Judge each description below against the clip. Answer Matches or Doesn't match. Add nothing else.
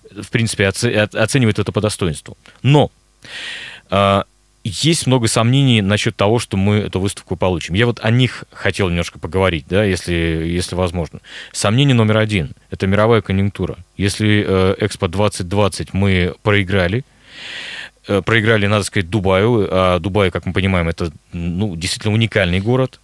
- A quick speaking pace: Doesn't match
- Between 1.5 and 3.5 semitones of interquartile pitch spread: Matches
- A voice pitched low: Matches